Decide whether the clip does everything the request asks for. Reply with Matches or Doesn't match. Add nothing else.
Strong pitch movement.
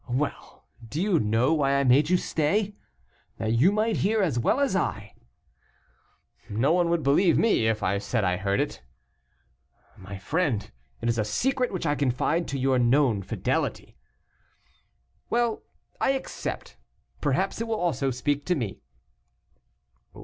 Matches